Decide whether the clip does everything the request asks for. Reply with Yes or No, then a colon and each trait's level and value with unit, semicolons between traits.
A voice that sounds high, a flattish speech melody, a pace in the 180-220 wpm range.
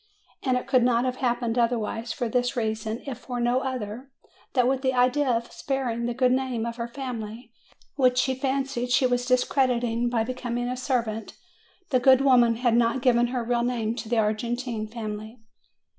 Yes: high, 245 Hz; narrow, 1.7 semitones; average, 185 wpm